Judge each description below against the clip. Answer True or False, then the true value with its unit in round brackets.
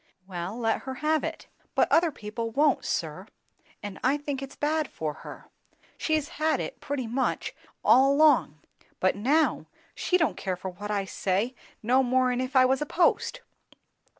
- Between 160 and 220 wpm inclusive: True (170 wpm)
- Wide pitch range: True (6.1 semitones)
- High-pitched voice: True (260 Hz)